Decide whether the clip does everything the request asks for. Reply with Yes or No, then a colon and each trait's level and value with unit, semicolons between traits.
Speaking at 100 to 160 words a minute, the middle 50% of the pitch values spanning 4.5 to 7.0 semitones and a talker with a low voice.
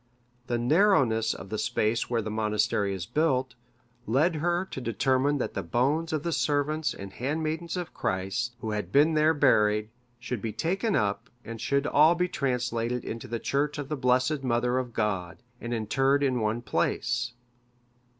No: average, 170 wpm; average, 5.0 semitones; low, 125 Hz